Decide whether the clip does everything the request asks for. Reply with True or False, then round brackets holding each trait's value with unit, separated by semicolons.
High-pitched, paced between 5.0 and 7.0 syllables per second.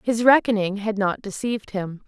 True (210 Hz; 5.1 syllables/s)